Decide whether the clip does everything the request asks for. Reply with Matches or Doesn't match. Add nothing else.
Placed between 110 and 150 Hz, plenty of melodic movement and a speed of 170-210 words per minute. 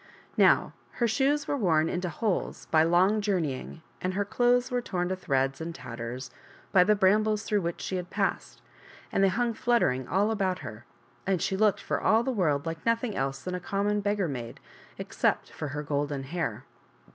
Doesn't match